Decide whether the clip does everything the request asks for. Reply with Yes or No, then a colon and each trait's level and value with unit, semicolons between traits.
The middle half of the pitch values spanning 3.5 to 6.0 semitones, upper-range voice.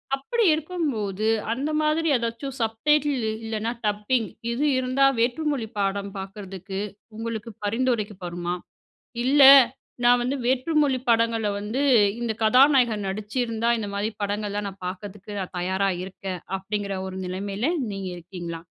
Yes: average, 4.3 semitones; high, 220 Hz